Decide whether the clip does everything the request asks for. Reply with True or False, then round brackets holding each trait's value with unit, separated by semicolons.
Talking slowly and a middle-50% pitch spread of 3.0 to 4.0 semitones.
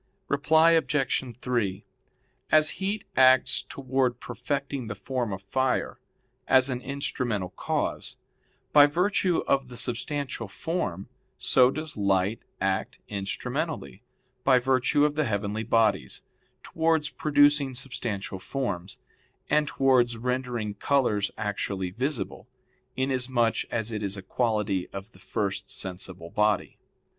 False (120 wpm; 5.2 semitones)